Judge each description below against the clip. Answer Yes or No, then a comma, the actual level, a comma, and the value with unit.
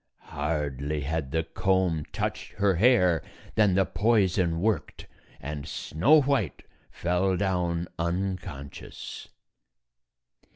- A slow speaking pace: Yes, slow, 100 wpm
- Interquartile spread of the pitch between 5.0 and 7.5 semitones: No, average, 4.0 semitones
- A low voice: Yes, very low, 90 Hz